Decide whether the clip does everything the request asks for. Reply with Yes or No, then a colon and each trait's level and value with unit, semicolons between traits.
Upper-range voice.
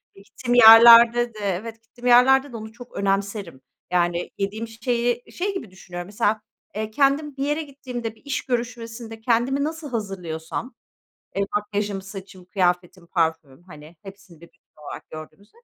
Yes: high, 220 Hz